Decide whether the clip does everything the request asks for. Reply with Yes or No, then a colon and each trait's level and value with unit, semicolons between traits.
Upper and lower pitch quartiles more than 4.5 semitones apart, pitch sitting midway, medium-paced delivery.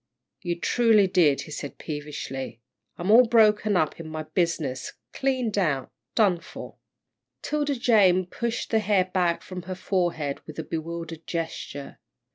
Yes: average, 5.0 semitones; medium, 175 Hz; average, 145 wpm